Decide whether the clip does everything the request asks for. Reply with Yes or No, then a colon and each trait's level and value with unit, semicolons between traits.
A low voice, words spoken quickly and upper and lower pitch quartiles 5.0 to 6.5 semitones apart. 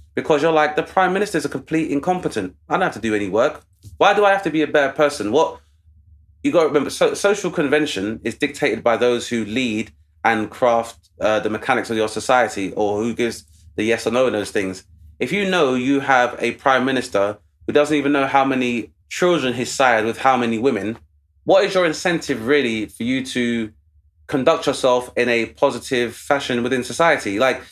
Yes: low, 125 Hz; fast, 210 wpm; wide, 5.5 semitones